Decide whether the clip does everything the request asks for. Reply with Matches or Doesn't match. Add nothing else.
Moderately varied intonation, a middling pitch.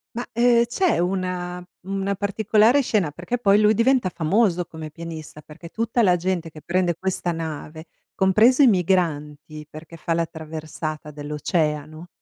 Matches